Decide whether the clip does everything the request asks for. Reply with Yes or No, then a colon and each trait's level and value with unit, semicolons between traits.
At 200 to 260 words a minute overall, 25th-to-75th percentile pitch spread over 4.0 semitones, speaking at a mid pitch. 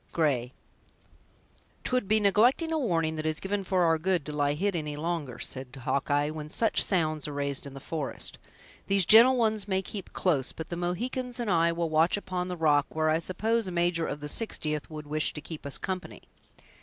Yes: fast, 205 wpm; average, 4.5 semitones; medium, 165 Hz